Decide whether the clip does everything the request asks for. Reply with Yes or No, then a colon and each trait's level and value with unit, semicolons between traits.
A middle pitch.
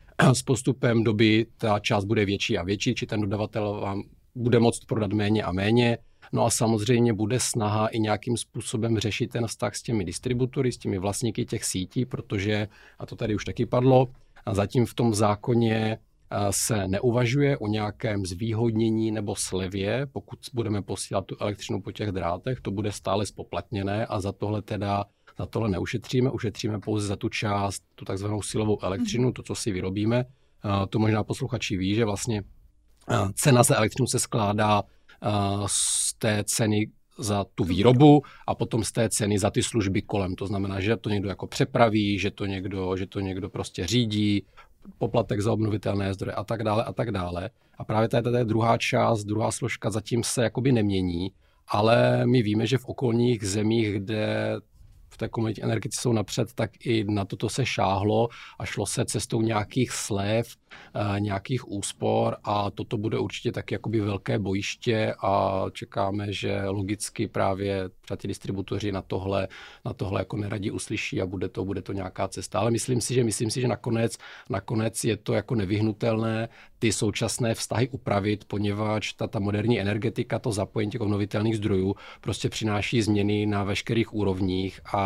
No: low, 110 Hz